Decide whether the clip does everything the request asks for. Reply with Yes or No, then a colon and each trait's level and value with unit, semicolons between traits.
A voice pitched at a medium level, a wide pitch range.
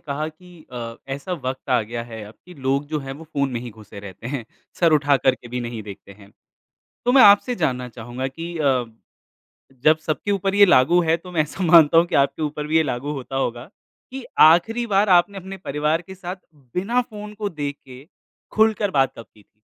Yes: medium, 150 Hz; wide, 6.0 semitones